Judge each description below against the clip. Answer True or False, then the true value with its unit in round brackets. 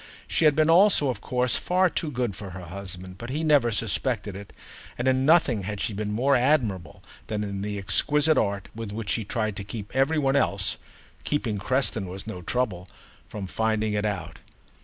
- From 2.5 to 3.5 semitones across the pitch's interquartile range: False (5.1 semitones)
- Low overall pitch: True (110 Hz)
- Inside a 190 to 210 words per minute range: True (195 wpm)